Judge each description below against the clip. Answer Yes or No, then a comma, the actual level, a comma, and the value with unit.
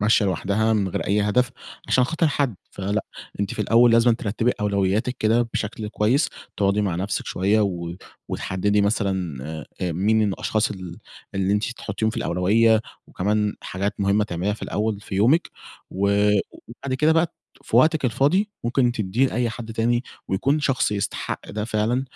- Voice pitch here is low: Yes, low, 105 Hz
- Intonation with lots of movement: No, average, 3.3 semitones